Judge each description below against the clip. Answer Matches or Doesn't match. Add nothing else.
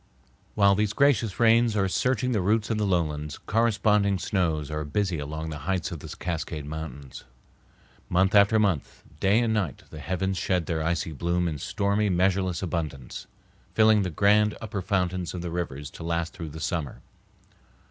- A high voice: Doesn't match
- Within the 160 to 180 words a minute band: Matches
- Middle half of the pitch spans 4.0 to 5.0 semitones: Matches